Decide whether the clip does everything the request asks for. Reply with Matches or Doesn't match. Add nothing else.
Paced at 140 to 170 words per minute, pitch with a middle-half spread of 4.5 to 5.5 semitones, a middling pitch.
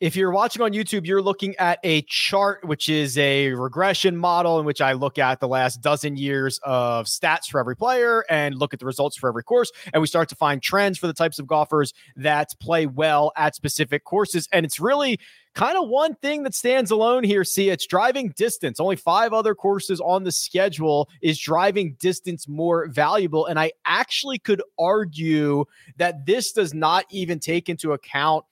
Doesn't match